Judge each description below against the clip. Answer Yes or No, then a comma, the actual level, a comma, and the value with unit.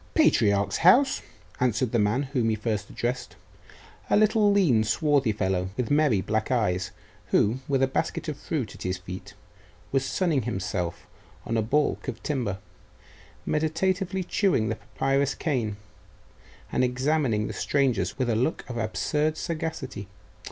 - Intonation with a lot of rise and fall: Yes, wide, 6.0 semitones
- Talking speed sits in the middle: Yes, average, 145 wpm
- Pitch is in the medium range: No, low, 125 Hz